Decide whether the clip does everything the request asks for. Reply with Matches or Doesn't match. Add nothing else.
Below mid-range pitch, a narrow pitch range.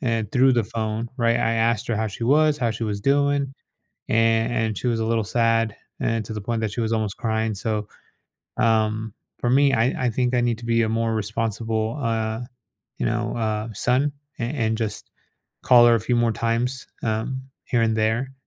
Matches